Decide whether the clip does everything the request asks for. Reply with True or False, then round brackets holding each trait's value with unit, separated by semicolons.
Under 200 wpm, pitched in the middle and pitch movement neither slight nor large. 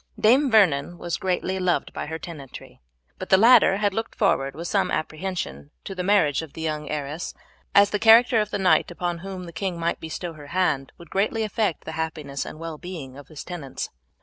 False (205 wpm; 175 Hz; 4.1 semitones)